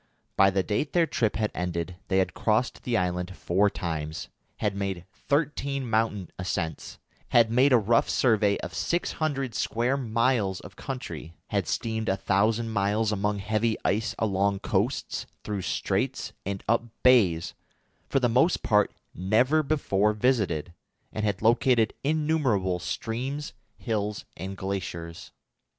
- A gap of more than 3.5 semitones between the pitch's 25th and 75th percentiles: Yes, average, 4.4 semitones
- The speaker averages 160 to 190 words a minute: No, average, 140 wpm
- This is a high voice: No, low, 105 Hz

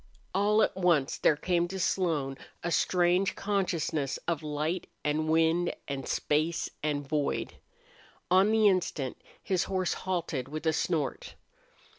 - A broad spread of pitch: No, average, 3.6 semitones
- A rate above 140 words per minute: No, slow, 135 wpm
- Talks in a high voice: No, medium, 170 Hz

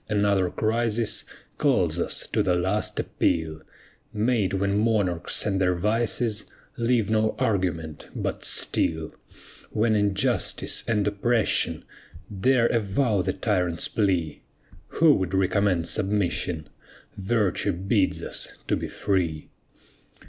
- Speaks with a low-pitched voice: Yes, low, 100 Hz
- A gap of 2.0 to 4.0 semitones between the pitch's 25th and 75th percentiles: Yes, average, 3.4 semitones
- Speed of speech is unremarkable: No, slow, 110 wpm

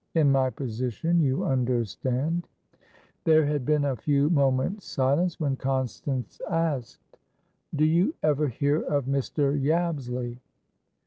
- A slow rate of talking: Yes, slow, 120 wpm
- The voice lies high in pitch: No, medium, 140 Hz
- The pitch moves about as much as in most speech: Yes, average, 3.2 semitones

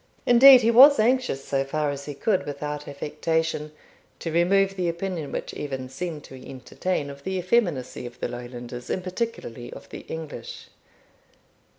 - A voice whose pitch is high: No, medium, 155 Hz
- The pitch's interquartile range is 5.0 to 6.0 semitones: Yes, wide, 5.6 semitones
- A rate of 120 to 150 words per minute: No, average, 160 wpm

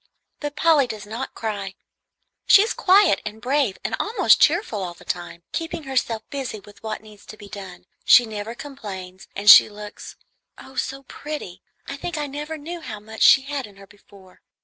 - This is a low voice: No, high, 225 Hz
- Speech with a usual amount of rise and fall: No, wide, 5.9 semitones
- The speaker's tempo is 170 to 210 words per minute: Yes, average, 190 wpm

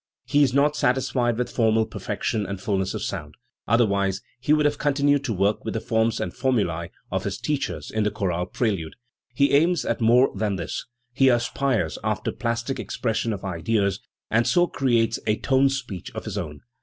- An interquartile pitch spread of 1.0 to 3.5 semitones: No, average, 5.2 semitones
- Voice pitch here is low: Yes, low, 115 Hz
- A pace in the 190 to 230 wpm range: Yes, average, 195 wpm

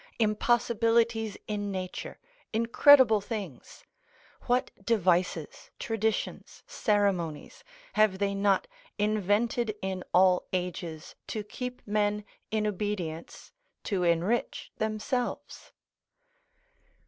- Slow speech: Yes, slow, 85 wpm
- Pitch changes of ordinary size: Yes, average, 3.1 semitones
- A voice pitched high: Yes, high, 210 Hz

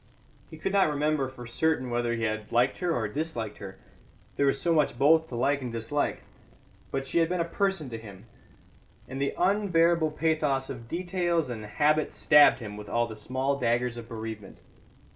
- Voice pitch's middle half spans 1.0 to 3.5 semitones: No, wide, 5.4 semitones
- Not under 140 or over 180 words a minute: No, average, 190 wpm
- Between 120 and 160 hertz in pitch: Yes, low, 135 Hz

